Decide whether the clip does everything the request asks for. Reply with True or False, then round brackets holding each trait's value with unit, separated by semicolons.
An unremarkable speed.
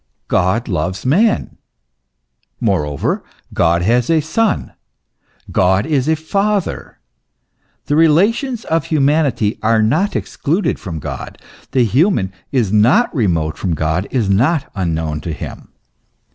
False (120 wpm)